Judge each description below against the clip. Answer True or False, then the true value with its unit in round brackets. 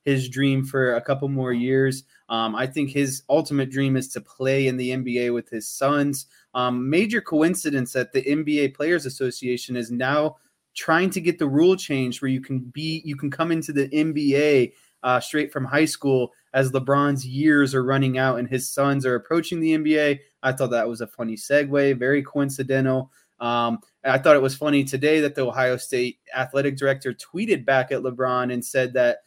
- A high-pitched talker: False (135 Hz)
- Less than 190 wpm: False (195 wpm)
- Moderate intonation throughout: False (2.2 semitones)